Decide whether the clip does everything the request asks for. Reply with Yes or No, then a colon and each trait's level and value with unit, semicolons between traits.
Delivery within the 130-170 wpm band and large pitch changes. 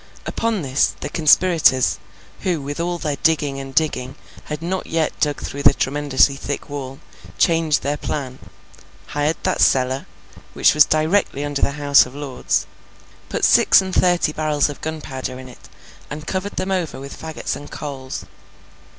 No: average, 160 wpm; average, 2.9 semitones